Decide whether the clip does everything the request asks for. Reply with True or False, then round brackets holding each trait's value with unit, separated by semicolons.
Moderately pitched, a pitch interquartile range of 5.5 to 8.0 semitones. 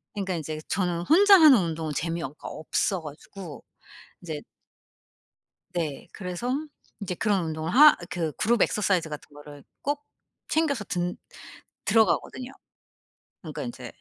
True (180 Hz; 6.0 semitones)